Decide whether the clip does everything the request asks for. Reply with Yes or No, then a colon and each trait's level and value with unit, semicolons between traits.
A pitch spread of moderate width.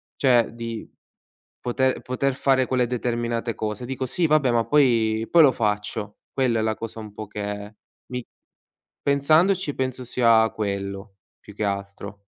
Yes: average, 3.7 semitones